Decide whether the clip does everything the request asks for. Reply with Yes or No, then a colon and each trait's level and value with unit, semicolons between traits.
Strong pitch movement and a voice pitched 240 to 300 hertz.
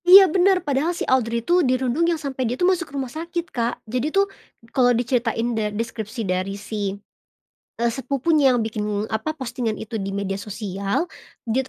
Yes: wide, 5.7 semitones; high, 245 Hz